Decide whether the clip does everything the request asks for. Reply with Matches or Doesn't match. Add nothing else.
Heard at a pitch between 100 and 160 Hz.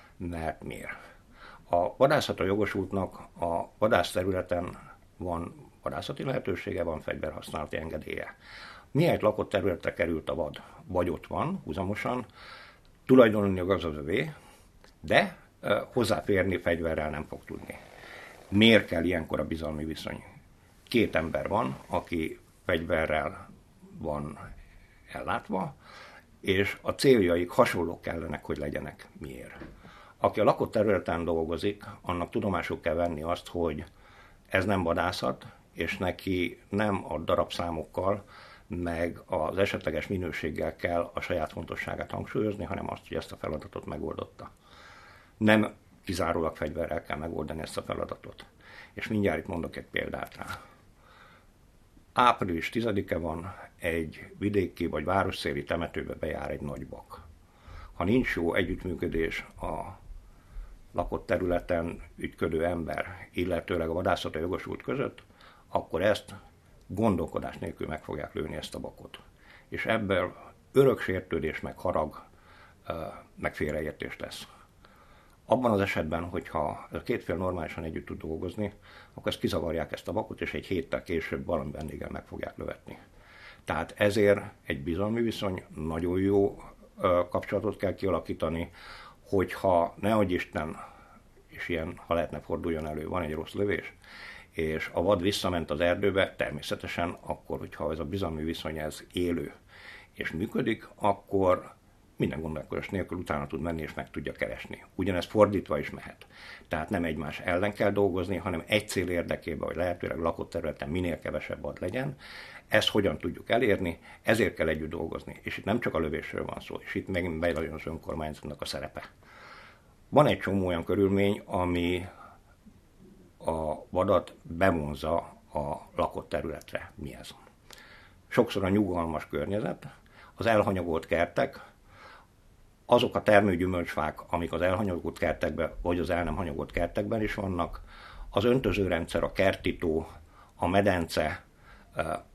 Doesn't match